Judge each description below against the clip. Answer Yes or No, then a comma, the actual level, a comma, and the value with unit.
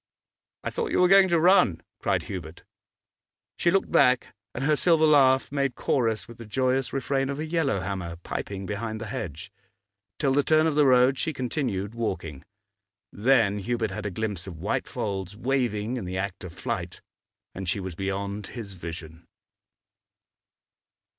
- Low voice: Yes, low, 115 Hz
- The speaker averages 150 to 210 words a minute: Yes, average, 165 wpm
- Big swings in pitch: Yes, wide, 6.0 semitones